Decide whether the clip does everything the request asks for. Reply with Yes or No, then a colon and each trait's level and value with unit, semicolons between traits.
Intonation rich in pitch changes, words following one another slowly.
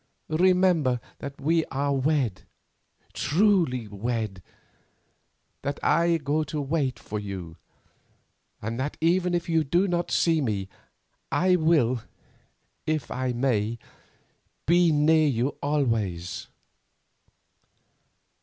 Yes: wide, 5.8 semitones; slow, 100 wpm